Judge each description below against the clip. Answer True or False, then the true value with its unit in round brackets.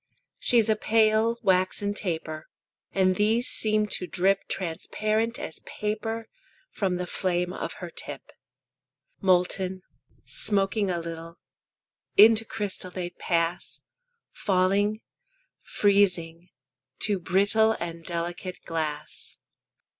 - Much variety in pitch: False (3.5 semitones)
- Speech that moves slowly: True (100 wpm)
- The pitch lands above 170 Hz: True (190 Hz)